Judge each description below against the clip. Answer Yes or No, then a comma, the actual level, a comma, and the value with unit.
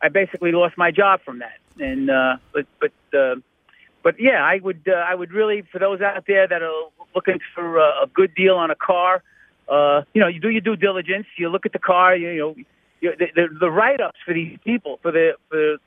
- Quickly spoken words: Yes, fast, 230 wpm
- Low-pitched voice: No, medium, 185 Hz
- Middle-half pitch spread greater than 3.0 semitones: Yes, average, 3.4 semitones